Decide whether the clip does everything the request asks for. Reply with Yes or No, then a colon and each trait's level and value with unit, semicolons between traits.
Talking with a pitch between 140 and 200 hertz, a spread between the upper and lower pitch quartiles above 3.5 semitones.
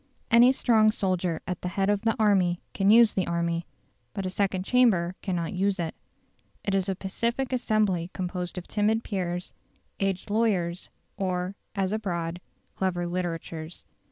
No: high, 190 Hz; average, 3.1 semitones